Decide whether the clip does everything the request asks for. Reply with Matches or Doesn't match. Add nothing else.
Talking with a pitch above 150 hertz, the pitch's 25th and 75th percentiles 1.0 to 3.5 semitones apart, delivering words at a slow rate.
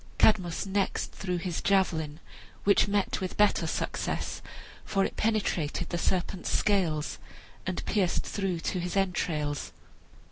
Matches